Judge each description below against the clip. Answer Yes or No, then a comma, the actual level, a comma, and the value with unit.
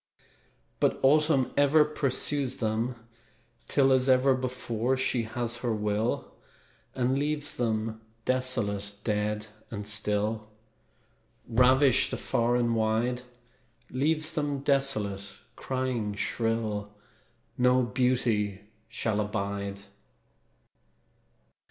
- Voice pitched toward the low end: Yes, low, 120 Hz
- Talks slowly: Yes, slow, 90 wpm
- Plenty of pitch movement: No, average, 3.6 semitones